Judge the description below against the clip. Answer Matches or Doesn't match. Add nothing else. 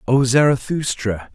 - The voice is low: Matches